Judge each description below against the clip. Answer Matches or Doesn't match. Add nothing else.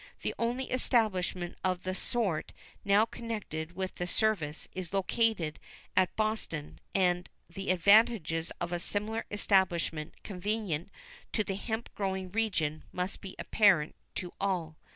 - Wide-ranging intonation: Doesn't match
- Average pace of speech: Doesn't match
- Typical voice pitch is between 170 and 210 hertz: Matches